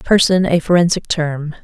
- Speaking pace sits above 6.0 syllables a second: No, 4.7 syllables/s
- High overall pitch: No, medium, 165 Hz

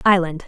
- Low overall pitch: No, medium, 175 Hz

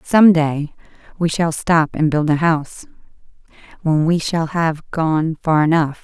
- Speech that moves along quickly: No, average, 160 wpm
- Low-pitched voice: No, medium, 160 Hz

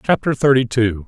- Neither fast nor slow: Yes, average, 170 wpm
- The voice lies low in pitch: Yes, low, 120 Hz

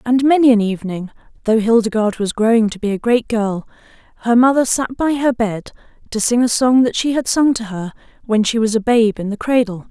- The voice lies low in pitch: No, high, 230 Hz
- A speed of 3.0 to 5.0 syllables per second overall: No, 5.6 syllables/s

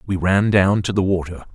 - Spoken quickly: Yes, fast, 235 wpm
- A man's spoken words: Yes, male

